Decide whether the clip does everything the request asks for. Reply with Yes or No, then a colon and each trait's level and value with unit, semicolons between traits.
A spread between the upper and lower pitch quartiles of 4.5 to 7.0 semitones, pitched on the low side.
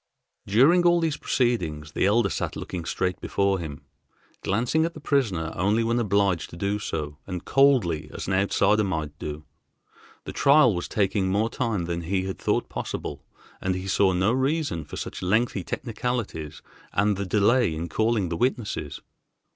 Yes: average, 5.3 semitones; low, 100 Hz